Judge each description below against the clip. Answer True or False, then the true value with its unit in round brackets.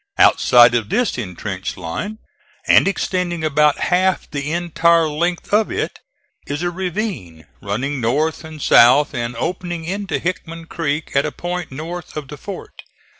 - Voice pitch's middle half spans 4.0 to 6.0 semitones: True (4.7 semitones)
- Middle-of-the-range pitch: True (160 Hz)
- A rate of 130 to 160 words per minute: True (150 wpm)